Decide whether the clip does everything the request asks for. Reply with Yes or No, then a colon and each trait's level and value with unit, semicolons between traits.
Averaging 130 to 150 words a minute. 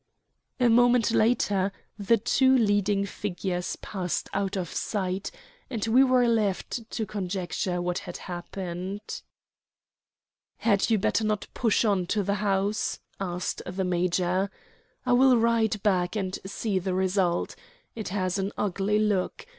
Yes: average, 140 wpm